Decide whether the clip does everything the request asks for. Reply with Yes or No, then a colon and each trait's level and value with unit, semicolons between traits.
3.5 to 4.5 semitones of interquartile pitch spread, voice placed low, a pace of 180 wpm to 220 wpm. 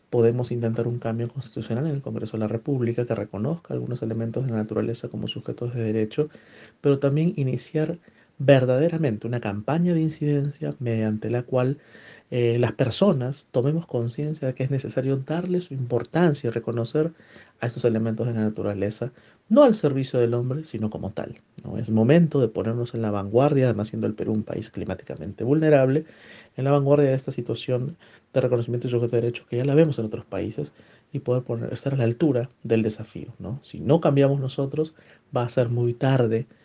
Yes: average, 3.8 semitones; low, 120 Hz; fast, 190 wpm